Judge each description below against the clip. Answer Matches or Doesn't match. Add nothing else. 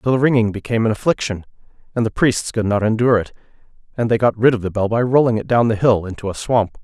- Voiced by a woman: Doesn't match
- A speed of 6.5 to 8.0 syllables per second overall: Matches